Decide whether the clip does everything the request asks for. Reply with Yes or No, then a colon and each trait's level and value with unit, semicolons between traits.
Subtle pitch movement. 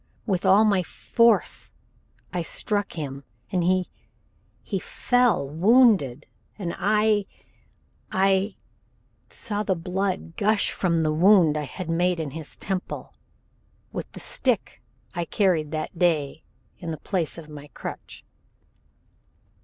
No: average, 4.0 semitones